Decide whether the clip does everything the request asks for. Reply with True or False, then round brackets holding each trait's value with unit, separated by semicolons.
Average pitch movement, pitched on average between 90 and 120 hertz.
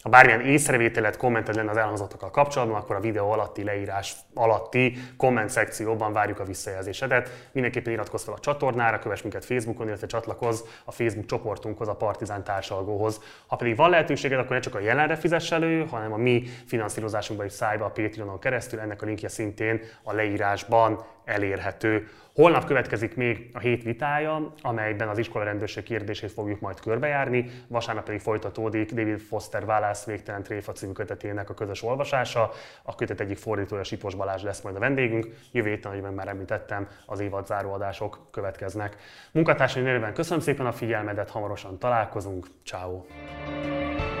True (3.1 semitones; 110 Hz)